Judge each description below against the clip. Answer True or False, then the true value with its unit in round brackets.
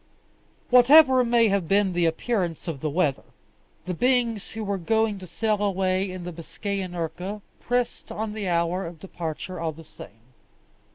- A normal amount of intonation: True (4.4 semitones)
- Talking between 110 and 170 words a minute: True (165 wpm)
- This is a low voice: False (190 Hz)